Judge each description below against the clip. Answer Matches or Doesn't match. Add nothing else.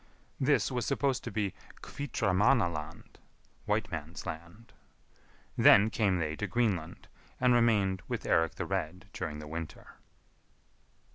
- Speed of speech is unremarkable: Doesn't match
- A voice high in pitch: Doesn't match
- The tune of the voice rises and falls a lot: Matches